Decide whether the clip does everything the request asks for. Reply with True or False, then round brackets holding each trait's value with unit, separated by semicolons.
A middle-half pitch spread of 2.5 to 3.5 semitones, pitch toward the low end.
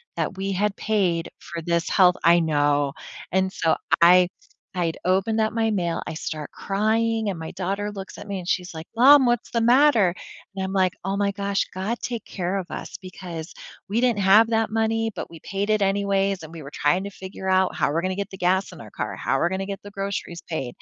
False (3.1 semitones; 190 Hz)